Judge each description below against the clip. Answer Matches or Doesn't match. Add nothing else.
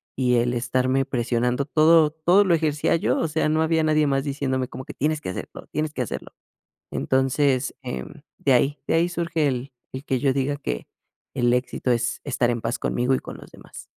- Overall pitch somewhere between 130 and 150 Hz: Matches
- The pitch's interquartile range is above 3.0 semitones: Matches